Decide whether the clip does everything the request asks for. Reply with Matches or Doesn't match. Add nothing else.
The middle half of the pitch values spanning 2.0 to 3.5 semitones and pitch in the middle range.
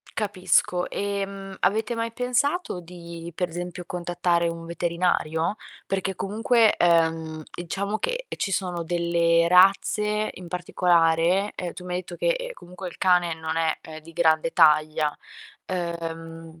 Matches